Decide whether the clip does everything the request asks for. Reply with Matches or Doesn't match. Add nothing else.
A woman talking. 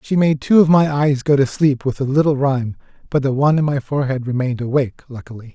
Doesn't match